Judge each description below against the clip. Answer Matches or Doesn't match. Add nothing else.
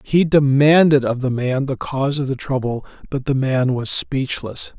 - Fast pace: Doesn't match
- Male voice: Matches